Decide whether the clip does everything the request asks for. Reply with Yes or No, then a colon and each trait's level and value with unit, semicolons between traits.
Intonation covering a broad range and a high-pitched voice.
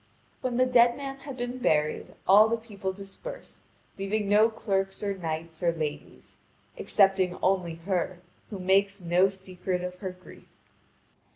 No: average, 3.3 semitones; high, 195 Hz